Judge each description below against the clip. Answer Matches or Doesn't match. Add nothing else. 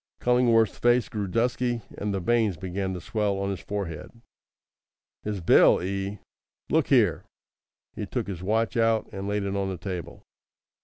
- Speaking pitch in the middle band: Doesn't match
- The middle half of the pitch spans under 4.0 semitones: Matches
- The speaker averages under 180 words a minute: Matches